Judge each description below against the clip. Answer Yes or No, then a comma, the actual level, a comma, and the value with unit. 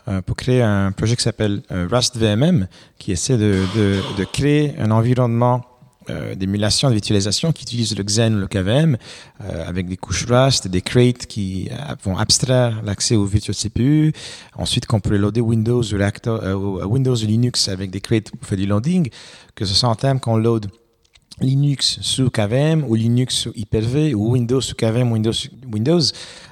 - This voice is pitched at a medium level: No, low, 115 Hz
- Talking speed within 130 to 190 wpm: Yes, average, 180 wpm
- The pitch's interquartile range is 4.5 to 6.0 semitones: No, average, 3.8 semitones